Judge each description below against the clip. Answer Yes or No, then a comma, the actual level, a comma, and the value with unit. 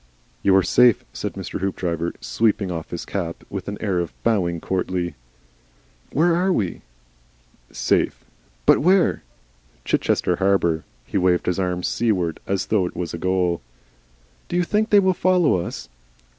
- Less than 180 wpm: Yes, average, 155 wpm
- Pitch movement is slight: No, average, 4.9 semitones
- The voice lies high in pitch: No, very low, 95 Hz